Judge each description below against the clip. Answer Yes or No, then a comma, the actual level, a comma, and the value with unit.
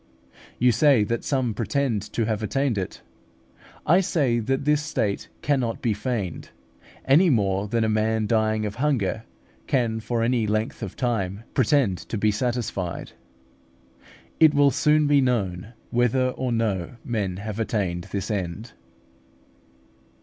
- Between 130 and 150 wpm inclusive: Yes, average, 140 wpm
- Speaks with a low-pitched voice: Yes, low, 115 Hz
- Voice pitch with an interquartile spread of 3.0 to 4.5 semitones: Yes, average, 3.8 semitones